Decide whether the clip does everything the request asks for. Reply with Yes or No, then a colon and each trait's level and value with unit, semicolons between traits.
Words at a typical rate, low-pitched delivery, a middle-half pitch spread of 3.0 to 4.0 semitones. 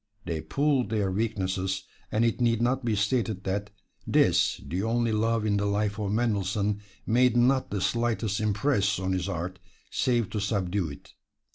Yes: average, 165 wpm; low, 105 Hz; average, 3.3 semitones